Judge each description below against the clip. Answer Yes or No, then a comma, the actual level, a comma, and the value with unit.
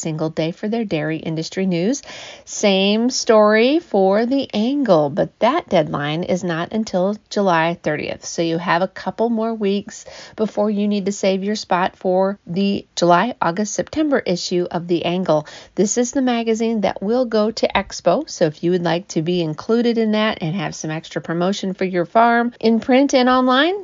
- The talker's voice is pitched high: Yes, high, 200 Hz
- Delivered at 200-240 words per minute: No, average, 185 wpm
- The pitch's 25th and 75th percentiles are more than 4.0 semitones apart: Yes, average, 4.8 semitones